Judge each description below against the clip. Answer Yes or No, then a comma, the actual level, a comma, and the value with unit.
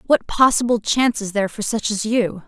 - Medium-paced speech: No, fast, 220 wpm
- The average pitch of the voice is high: Yes, high, 220 Hz